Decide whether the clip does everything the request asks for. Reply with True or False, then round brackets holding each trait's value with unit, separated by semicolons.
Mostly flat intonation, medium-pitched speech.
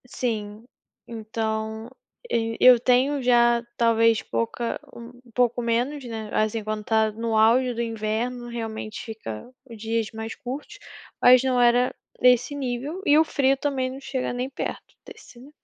False (2.2 semitones; 235 Hz)